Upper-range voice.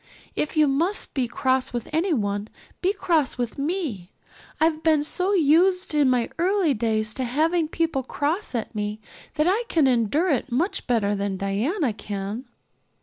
Yes: very high, 280 Hz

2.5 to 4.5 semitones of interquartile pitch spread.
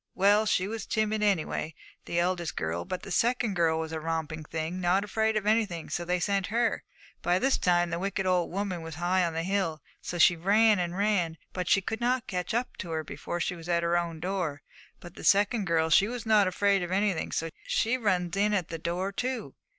Yes: average, 3.5 semitones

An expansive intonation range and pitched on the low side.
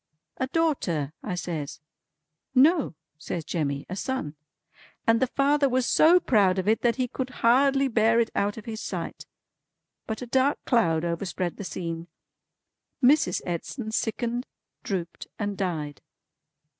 No: wide, 6.8 semitones; high, 220 Hz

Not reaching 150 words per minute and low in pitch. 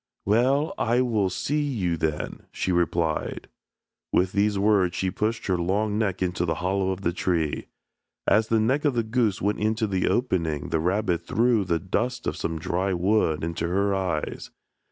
No: average, 175 wpm; very low, 95 Hz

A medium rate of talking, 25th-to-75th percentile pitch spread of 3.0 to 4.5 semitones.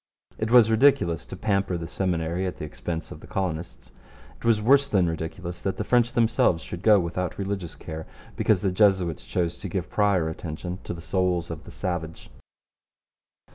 Yes: average, 180 wpm; average, 3.5 semitones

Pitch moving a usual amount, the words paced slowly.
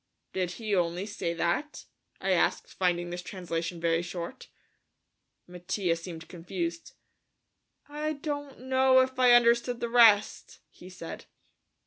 No: wide, 6.2 semitones; slow, 125 wpm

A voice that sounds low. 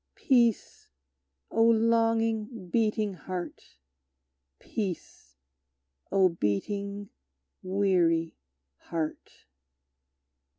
No: high, 200 Hz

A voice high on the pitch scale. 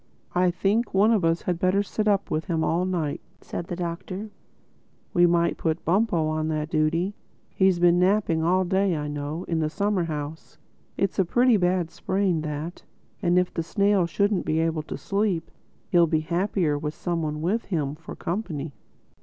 No: medium, 175 Hz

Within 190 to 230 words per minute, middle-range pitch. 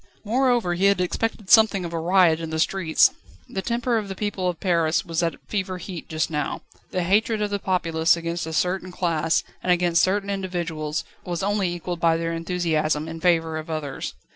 Yes: average, 195 wpm; medium, 175 Hz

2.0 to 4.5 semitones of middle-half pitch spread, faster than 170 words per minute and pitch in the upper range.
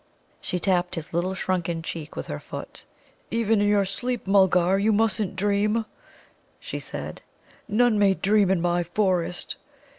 No: average, 2.9 semitones; average, 150 wpm; high, 195 Hz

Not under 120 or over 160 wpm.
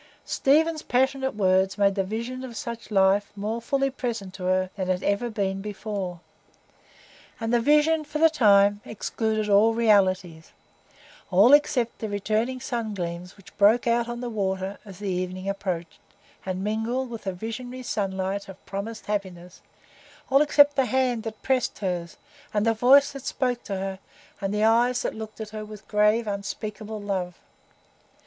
No: average, 170 wpm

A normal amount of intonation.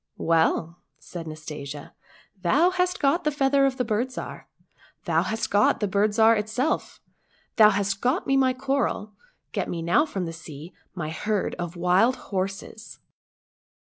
No: wide, 7.0 semitones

